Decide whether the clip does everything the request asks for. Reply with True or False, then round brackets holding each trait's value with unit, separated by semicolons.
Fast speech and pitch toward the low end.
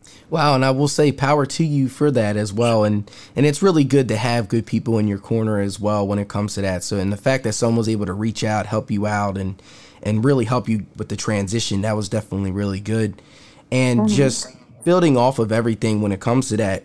True (245 wpm; 110 Hz)